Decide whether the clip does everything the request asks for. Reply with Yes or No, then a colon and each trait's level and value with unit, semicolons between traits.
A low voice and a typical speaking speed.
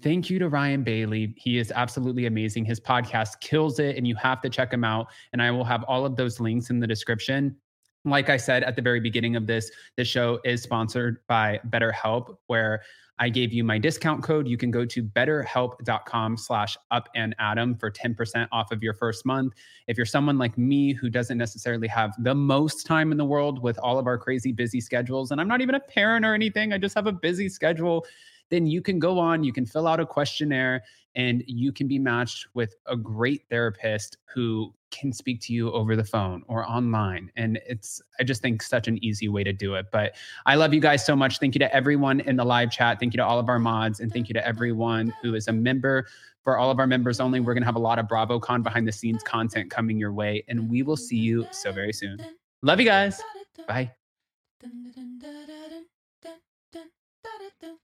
No: low, 125 Hz; fast, 220 wpm